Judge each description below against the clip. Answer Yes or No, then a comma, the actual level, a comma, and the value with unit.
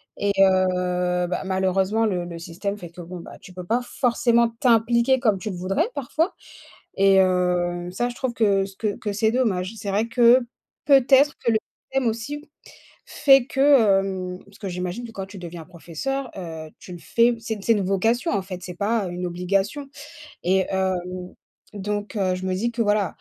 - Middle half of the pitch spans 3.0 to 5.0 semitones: Yes, average, 4.3 semitones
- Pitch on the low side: No, high, 195 Hz